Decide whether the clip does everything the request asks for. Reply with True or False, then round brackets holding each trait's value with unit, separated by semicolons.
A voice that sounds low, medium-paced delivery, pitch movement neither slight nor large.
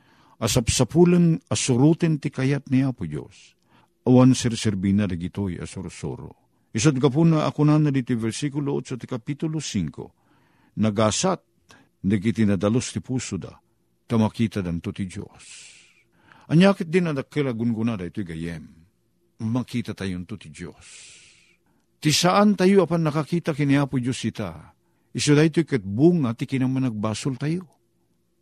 False (125 Hz; 130 wpm; 5.8 semitones)